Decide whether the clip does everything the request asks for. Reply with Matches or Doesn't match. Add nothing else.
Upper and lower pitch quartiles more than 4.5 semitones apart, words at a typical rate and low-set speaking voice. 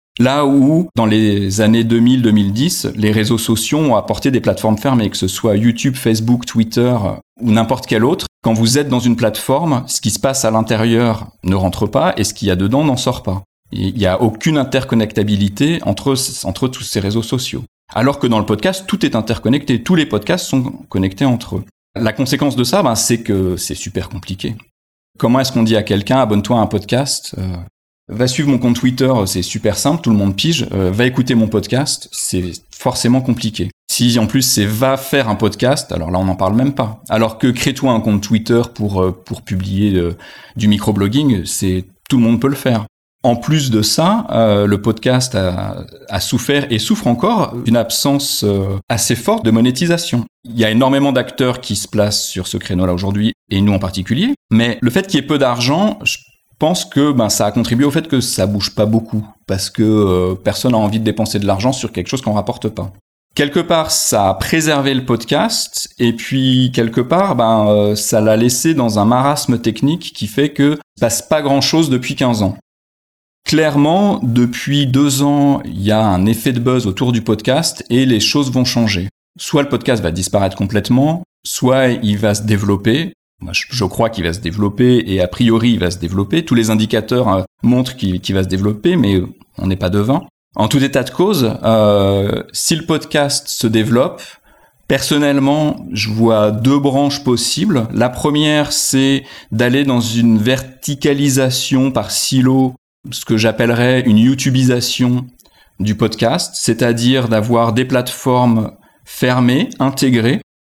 Doesn't match